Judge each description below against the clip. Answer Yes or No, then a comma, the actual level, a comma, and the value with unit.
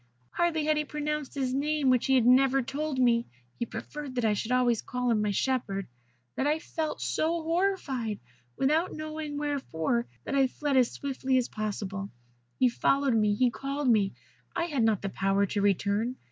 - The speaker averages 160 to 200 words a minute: Yes, average, 185 wpm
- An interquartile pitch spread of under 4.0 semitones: No, average, 4.8 semitones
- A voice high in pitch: Yes, very high, 260 Hz